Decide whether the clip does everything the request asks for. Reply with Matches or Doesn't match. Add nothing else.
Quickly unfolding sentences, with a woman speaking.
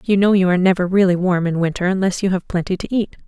Matches